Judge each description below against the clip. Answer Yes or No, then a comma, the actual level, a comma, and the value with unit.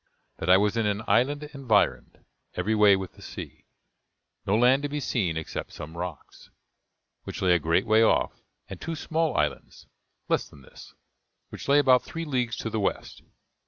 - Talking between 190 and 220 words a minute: No, average, 180 wpm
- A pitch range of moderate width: No, wide, 6.5 semitones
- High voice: No, low, 110 Hz